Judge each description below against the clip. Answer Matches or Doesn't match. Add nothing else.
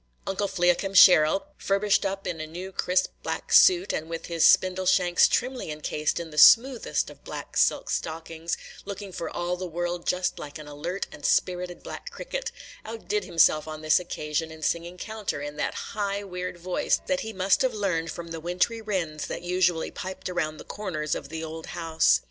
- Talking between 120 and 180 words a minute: Doesn't match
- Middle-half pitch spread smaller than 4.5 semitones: Matches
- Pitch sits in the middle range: Matches